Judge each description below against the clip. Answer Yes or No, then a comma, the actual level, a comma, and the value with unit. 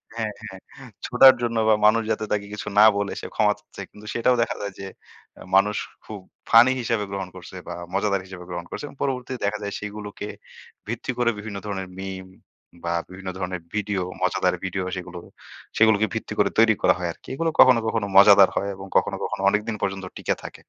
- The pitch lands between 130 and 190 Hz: No, low, 105 Hz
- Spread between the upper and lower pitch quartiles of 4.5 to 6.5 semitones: No, average, 2.8 semitones